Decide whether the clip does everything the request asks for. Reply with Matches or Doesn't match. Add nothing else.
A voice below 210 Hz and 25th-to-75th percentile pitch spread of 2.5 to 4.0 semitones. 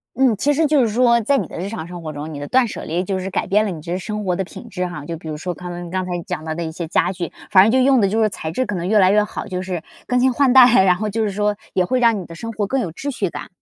Doesn't match